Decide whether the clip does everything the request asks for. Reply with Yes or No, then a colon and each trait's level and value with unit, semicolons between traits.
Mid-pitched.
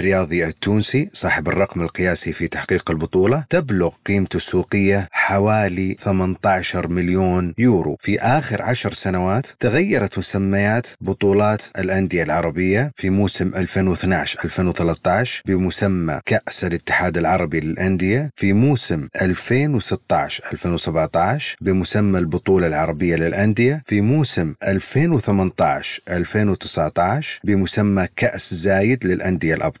No: very low, 95 Hz